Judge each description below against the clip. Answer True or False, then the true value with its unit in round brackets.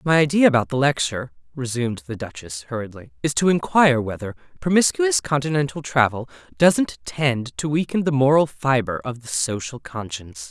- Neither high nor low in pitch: False (130 Hz)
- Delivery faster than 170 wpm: False (155 wpm)